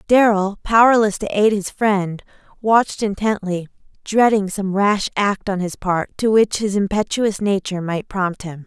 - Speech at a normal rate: Yes, average, 160 wpm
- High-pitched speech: Yes, high, 200 Hz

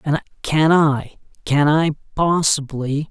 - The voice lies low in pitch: No, medium, 150 Hz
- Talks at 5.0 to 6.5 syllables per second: No, 3.5 syllables/s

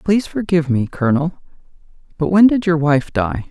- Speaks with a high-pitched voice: No, medium, 160 Hz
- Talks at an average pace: Yes, average, 170 wpm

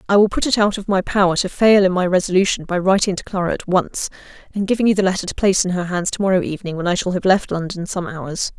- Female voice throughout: Yes, female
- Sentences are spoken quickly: Yes, fast, 280 wpm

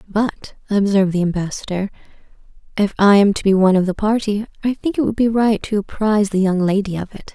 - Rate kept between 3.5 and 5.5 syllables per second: No, 6.0 syllables/s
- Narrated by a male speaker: No, female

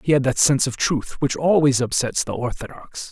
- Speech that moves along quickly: Yes, fast, 210 wpm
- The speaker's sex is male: Yes, male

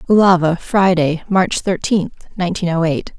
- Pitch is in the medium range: Yes, medium, 180 Hz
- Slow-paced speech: Yes, slow, 130 wpm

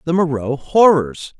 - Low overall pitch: No, medium, 150 Hz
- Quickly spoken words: No, slow, 130 wpm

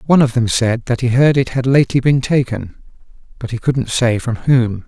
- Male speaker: Yes, male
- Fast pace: Yes, fast, 220 wpm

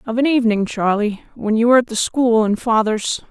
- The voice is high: Yes, high, 225 Hz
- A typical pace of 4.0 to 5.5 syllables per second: No, 5.7 syllables/s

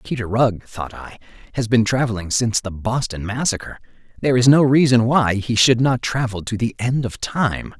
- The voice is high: No, low, 115 Hz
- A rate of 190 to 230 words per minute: Yes, average, 200 wpm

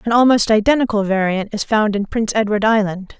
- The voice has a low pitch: No, high, 215 Hz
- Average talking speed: Yes, average, 190 wpm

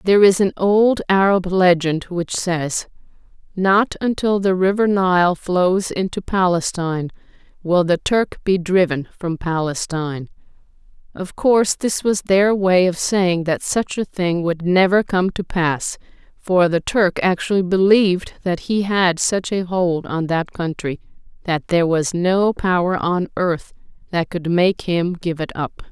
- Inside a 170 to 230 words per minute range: No, average, 155 wpm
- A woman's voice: Yes, female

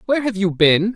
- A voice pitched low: No, high, 205 Hz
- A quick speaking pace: Yes, fast, 255 wpm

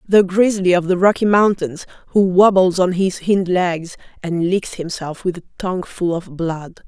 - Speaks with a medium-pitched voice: Yes, medium, 180 Hz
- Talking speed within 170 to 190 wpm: Yes, average, 185 wpm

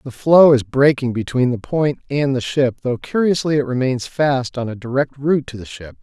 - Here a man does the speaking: Yes, male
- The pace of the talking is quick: Yes, fast, 220 wpm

